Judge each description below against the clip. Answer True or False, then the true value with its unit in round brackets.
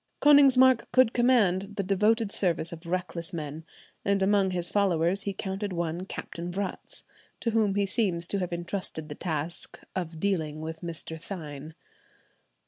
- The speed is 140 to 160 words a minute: True (150 wpm)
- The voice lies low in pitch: False (185 Hz)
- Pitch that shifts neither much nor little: True (3.3 semitones)